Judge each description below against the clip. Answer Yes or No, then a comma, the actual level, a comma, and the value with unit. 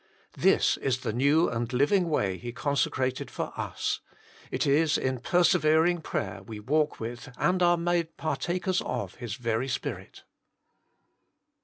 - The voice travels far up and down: Yes, wide, 5.7 semitones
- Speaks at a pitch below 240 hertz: Yes, medium, 140 Hz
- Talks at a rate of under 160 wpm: Yes, average, 140 wpm